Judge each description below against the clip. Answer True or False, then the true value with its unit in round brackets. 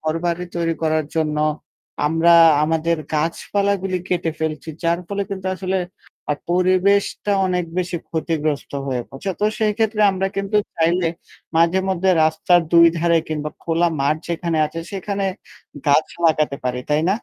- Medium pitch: True (170 Hz)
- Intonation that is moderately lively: True (3.0 semitones)